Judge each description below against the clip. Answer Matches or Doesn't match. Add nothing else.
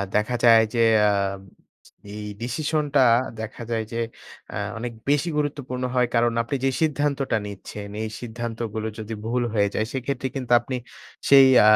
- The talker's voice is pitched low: Matches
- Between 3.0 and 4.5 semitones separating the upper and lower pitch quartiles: Matches